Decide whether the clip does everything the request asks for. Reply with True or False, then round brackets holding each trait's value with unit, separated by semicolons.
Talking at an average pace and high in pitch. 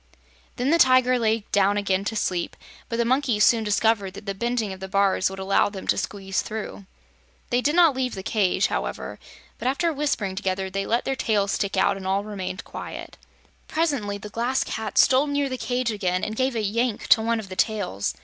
False (210 wpm; 215 Hz)